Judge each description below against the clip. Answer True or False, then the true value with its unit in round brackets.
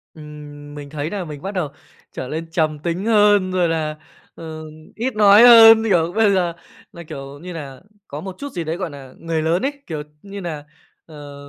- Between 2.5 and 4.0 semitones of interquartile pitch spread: False (4.6 semitones)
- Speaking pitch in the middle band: True (165 Hz)